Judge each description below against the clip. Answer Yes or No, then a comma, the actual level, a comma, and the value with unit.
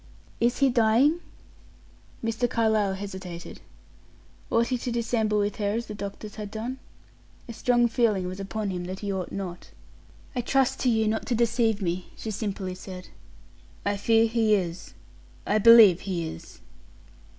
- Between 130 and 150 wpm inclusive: No, average, 160 wpm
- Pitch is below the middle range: No, high, 215 Hz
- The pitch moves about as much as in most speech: Yes, average, 3.2 semitones